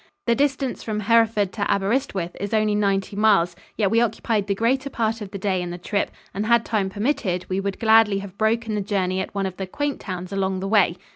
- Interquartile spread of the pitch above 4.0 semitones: No, average, 2.8 semitones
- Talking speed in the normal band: No, fast, 225 wpm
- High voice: Yes, high, 205 Hz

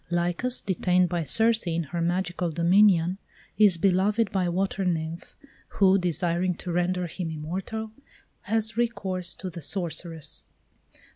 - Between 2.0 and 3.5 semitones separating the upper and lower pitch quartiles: Yes, narrow, 2.5 semitones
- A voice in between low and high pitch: Yes, medium, 180 Hz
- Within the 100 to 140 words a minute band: Yes, slow, 135 wpm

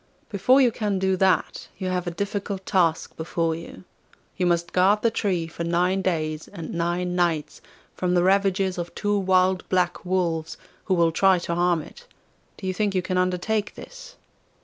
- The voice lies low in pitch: No, medium, 185 Hz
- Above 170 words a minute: Yes, average, 180 wpm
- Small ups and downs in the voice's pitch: Yes, narrow, 2.2 semitones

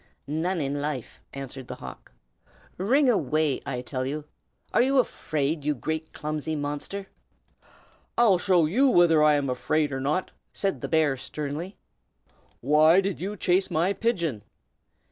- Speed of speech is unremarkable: Yes, average, 150 wpm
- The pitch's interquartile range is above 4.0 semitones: Yes, average, 4.5 semitones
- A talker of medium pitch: Yes, medium, 155 Hz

